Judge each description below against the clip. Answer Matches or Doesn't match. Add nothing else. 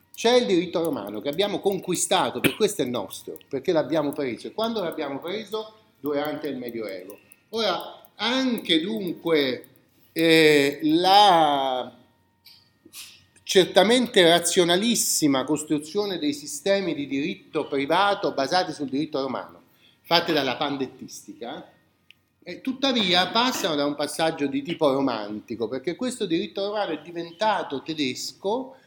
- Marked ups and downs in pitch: Matches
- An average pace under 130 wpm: Matches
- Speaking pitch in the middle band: Matches